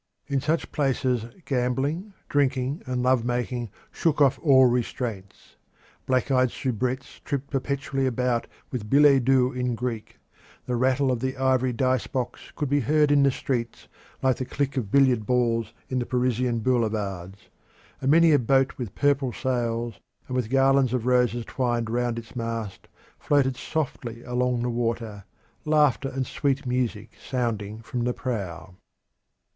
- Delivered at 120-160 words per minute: Yes, average, 150 wpm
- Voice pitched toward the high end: No, low, 125 Hz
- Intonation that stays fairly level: Yes, narrow, 2.3 semitones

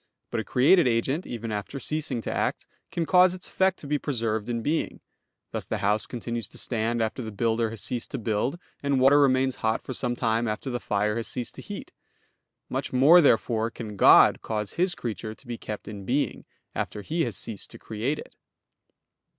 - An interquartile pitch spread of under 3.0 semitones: No, average, 4.0 semitones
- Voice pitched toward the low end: Yes, low, 120 Hz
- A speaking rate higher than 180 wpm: Yes, average, 200 wpm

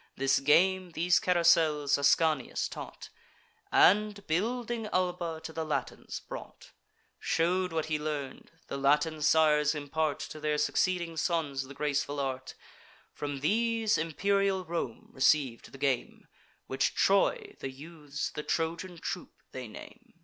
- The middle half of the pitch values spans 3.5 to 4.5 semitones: Yes, average, 3.9 semitones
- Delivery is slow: Yes, slow, 130 wpm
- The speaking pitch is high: No, medium, 160 Hz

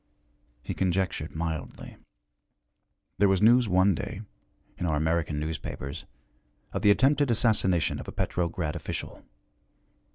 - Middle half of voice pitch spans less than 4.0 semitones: No, average, 4.3 semitones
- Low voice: Yes, very low, 90 Hz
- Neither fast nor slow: No, slow, 120 wpm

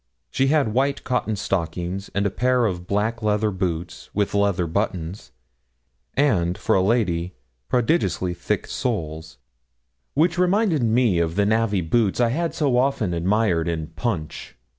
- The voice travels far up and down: Yes, wide, 5.8 semitones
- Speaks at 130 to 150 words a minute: Yes, average, 145 wpm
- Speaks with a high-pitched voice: No, low, 105 Hz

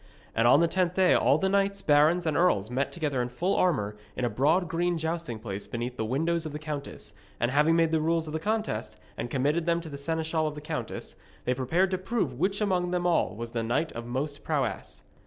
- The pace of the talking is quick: Yes, fast, 230 wpm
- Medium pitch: Yes, medium, 155 Hz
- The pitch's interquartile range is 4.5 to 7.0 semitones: Yes, wide, 5.4 semitones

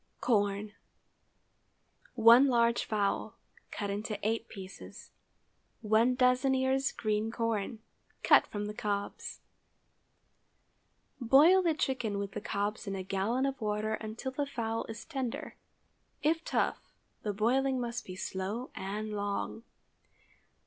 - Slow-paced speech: Yes, slow, 120 wpm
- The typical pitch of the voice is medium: No, high, 225 Hz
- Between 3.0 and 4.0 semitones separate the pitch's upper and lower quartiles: Yes, average, 3.6 semitones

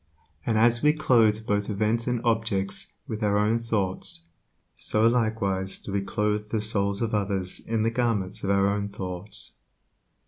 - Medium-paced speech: Yes, average, 160 wpm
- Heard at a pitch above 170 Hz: No, low, 105 Hz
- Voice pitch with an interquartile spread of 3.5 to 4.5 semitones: No, narrow, 2.4 semitones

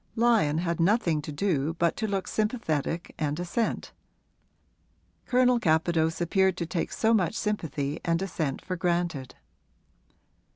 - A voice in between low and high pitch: Yes, medium, 170 Hz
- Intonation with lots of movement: No, average, 4.3 semitones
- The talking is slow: Yes, slow, 130 wpm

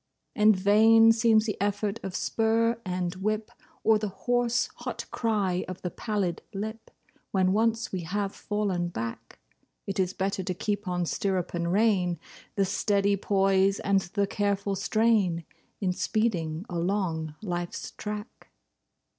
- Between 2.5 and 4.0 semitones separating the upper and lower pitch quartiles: Yes, average, 2.9 semitones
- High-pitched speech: Yes, high, 200 Hz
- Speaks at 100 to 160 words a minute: Yes, average, 140 wpm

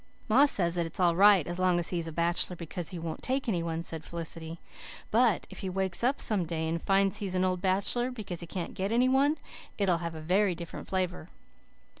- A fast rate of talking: Yes, fast, 235 wpm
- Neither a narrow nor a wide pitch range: Yes, average, 3.2 semitones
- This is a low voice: No, medium, 180 Hz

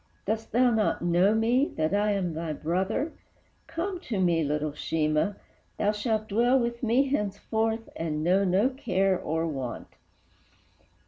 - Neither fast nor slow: Yes, average, 145 wpm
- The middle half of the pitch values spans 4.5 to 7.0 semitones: Yes, wide, 5.6 semitones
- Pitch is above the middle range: Yes, high, 205 Hz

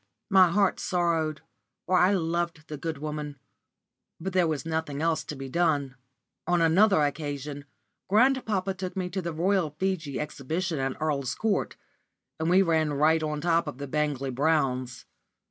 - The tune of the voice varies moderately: Yes, average, 3.5 semitones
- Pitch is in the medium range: Yes, medium, 160 Hz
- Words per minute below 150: No, average, 160 wpm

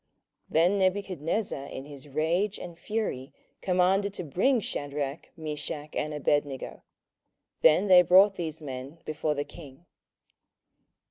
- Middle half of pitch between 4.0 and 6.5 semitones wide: Yes, average, 4.4 semitones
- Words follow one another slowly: Yes, slow, 125 wpm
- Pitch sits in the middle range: Yes, medium, 160 Hz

